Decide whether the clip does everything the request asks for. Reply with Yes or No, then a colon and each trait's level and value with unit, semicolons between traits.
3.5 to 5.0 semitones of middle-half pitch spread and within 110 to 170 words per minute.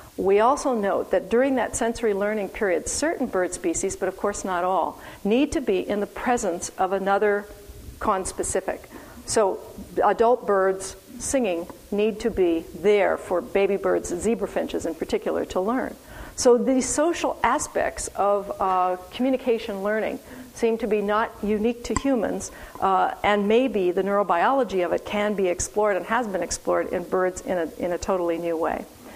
Yes: average, 4.0 semitones; average, 165 wpm